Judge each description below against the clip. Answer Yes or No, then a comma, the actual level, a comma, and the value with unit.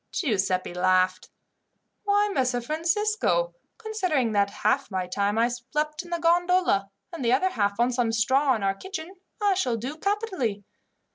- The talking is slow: No, average, 155 wpm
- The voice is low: No, very high, 260 Hz